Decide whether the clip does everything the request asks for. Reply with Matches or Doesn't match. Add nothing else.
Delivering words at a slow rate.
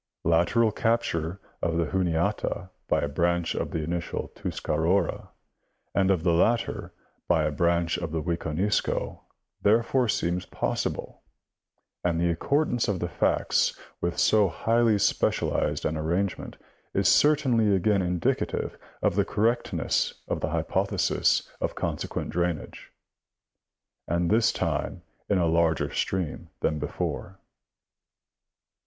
Matches